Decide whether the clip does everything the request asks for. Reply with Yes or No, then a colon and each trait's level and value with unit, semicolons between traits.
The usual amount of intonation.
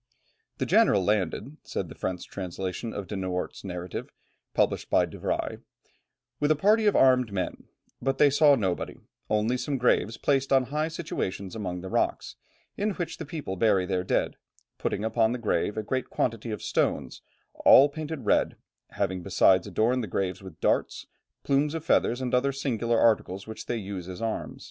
No: wide, 6.2 semitones